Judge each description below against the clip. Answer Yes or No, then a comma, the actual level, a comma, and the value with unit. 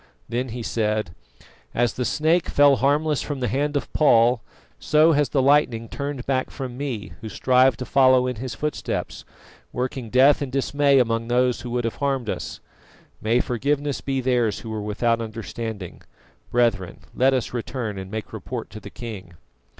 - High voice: No, low, 125 Hz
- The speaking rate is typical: Yes, average, 175 wpm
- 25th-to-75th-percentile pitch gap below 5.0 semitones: Yes, average, 3.2 semitones